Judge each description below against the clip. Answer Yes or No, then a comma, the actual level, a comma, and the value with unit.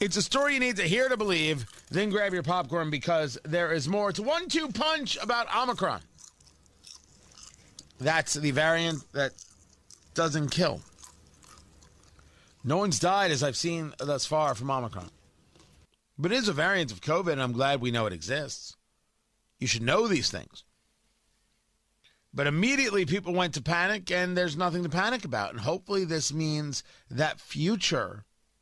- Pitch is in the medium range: Yes, medium, 155 Hz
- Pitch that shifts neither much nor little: No, wide, 7.5 semitones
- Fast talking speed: No, average, 160 wpm